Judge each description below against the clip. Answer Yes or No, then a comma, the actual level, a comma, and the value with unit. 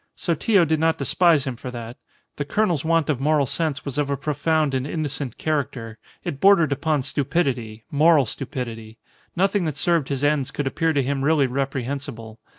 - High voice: No, medium, 145 Hz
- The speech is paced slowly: No, average, 175 wpm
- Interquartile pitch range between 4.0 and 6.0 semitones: No, average, 3.3 semitones